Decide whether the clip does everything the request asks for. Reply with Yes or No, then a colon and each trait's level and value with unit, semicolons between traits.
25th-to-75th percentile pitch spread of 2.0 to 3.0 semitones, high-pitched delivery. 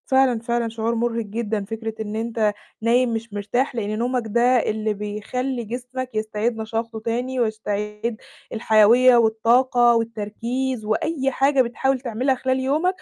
Yes: narrow, 2.5 semitones; high, 230 Hz